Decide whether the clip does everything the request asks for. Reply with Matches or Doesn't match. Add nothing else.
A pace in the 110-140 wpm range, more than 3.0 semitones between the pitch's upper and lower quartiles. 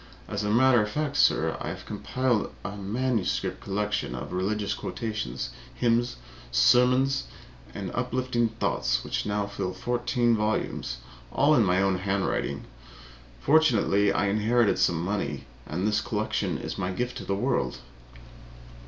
Matches